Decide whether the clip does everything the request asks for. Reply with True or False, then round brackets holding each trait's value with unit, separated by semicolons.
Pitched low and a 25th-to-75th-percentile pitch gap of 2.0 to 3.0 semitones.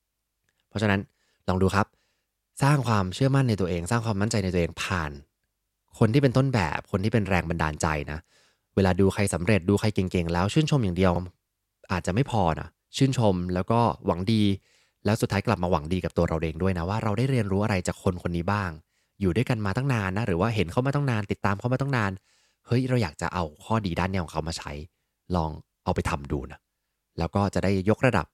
False (100 Hz; 4.1 semitones)